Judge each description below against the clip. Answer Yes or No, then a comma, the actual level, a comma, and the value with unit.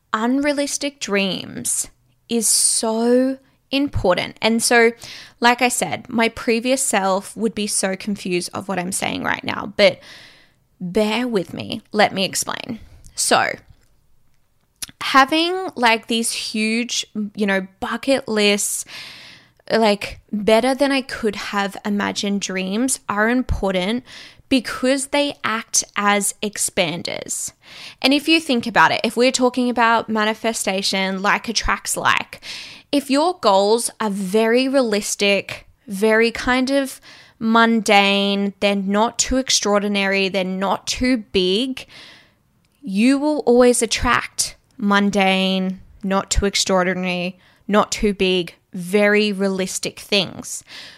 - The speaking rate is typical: No, slow, 120 wpm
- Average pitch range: Yes, average, 3.9 semitones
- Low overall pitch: No, high, 220 Hz